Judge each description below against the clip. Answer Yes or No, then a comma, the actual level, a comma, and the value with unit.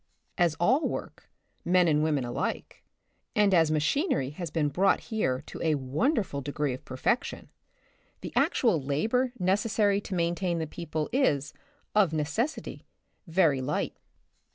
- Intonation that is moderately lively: No, wide, 5.7 semitones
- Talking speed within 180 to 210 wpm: No, average, 140 wpm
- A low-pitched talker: No, medium, 170 Hz